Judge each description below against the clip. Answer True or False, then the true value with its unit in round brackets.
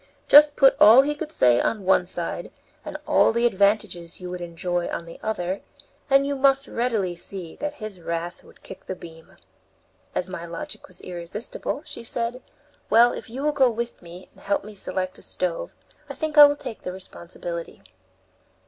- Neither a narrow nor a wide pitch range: False (7.2 semitones)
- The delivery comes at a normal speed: True (185 wpm)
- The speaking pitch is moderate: False (205 Hz)